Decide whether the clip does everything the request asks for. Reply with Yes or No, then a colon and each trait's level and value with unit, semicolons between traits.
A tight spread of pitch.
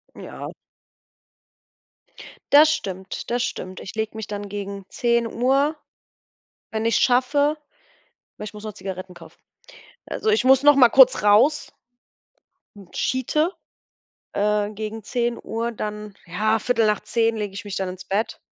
No: average, 3.6 semitones